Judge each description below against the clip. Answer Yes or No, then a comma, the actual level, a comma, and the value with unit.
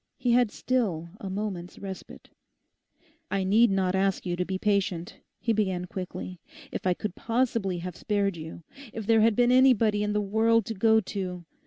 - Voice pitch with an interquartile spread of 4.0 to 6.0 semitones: No, average, 3.5 semitones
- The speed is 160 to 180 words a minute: Yes, average, 175 wpm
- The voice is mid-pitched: No, high, 200 Hz